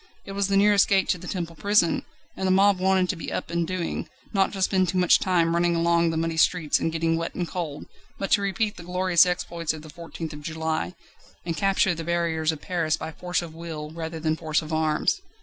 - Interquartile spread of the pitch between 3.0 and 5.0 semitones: No, narrow, 2.5 semitones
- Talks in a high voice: No, medium, 170 Hz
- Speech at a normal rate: No, fast, 235 wpm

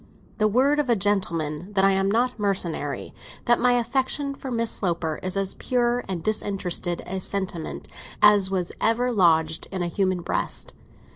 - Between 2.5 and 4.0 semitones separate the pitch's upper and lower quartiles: No, average, 5.1 semitones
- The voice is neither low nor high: No, high, 195 Hz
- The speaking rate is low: No, average, 165 wpm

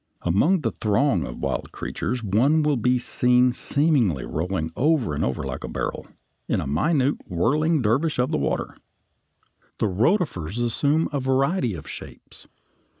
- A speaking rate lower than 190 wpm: Yes, average, 150 wpm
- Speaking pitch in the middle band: No, low, 125 Hz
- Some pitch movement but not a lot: No, wide, 7.4 semitones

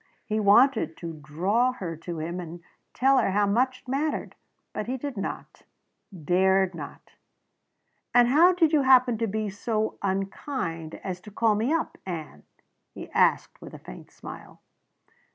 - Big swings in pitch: Yes, wide, 6.2 semitones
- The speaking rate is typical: Yes, average, 160 wpm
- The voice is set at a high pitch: Yes, high, 210 Hz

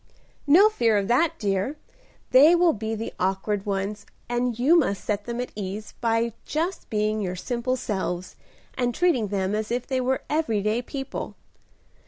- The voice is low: No, high, 230 Hz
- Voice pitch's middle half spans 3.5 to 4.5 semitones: Yes, average, 4.0 semitones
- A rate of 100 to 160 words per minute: No, average, 170 wpm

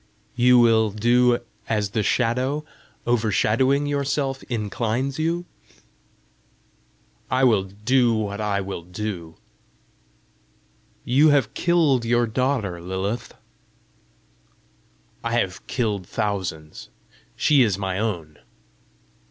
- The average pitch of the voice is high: No, low, 115 Hz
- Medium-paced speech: No, slow, 105 wpm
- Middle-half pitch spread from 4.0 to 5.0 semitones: Yes, average, 4.3 semitones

